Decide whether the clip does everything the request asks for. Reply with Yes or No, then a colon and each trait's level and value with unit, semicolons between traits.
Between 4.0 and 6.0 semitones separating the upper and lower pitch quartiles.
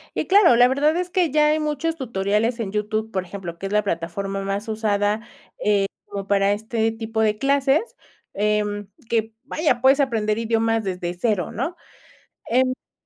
Yes: average, 4.6 semitones